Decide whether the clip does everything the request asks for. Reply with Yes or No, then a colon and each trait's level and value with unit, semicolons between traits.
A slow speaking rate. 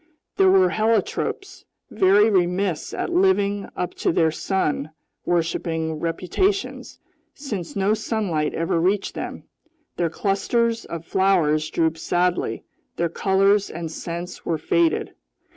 Yes: slow, 120 wpm